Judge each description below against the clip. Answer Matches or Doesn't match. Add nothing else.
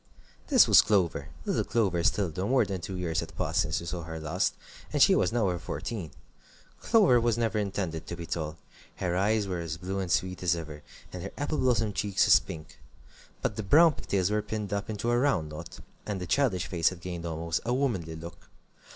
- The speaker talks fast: Matches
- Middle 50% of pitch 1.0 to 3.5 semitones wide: Doesn't match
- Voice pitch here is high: Doesn't match